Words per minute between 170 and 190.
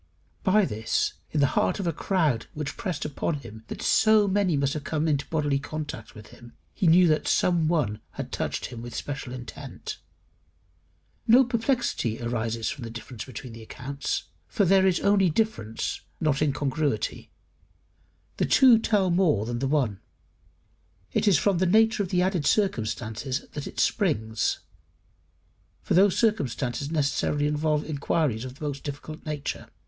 No: average, 160 wpm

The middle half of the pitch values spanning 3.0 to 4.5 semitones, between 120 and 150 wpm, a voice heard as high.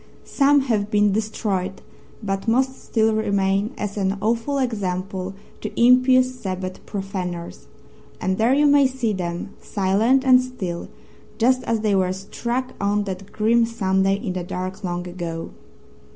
Yes: average, 4.0 semitones; average, 145 wpm; high, 205 Hz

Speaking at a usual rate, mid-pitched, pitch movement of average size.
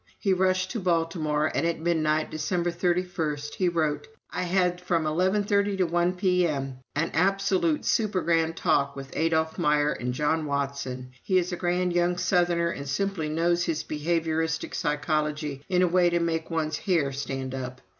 Yes: average, 165 wpm; medium, 165 Hz; average, 3.0 semitones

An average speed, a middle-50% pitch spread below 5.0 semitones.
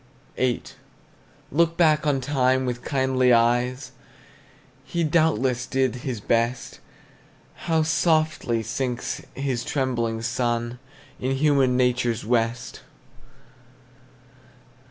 No: slow, 95 wpm; average, 2.9 semitones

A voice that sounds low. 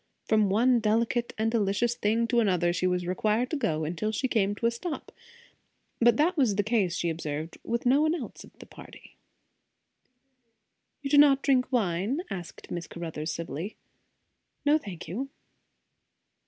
No: high, 215 Hz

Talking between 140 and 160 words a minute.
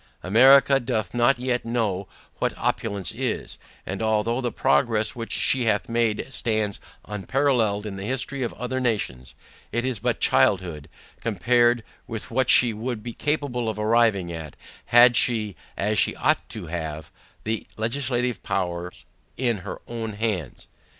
Yes: average, 150 wpm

